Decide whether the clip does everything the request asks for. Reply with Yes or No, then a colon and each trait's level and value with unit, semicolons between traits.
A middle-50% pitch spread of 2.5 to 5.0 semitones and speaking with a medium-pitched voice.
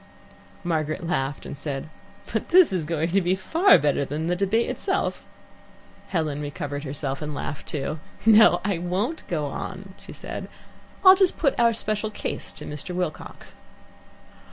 No: wide, 5.5 semitones; medium, 175 Hz